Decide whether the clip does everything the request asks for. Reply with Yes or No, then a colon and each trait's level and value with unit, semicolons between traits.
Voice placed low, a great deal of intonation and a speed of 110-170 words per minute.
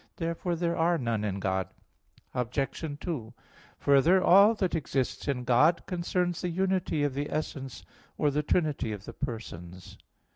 No: medium, 145 Hz; wide, 6.0 semitones; average, 150 wpm